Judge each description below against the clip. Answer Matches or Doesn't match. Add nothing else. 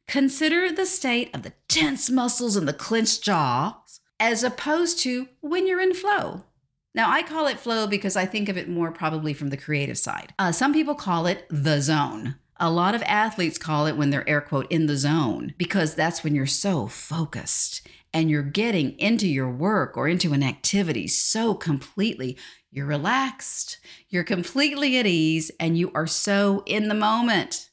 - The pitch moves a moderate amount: Doesn't match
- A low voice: Doesn't match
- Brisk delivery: Doesn't match